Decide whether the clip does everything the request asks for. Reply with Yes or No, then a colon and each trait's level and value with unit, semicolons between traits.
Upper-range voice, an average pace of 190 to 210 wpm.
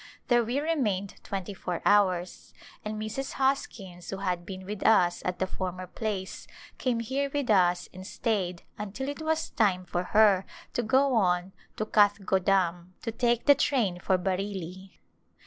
No: high, 200 Hz; average, 165 wpm